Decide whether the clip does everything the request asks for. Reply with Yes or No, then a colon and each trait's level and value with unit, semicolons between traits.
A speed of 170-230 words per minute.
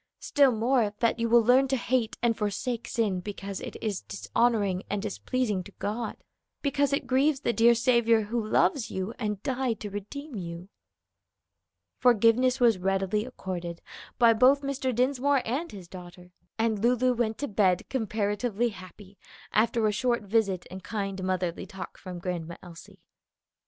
No: average, 155 wpm